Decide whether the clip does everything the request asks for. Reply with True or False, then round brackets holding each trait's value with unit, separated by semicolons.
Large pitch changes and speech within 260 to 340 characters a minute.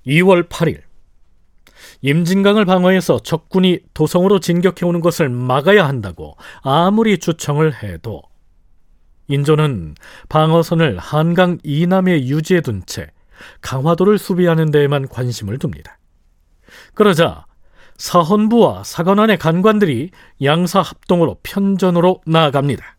True (6.6 semitones; 265 characters per minute)